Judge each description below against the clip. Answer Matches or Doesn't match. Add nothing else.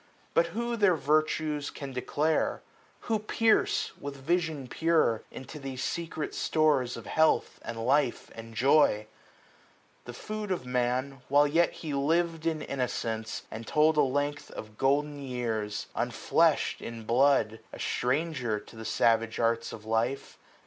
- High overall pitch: Doesn't match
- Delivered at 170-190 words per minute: Doesn't match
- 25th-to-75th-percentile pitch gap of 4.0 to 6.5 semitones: Matches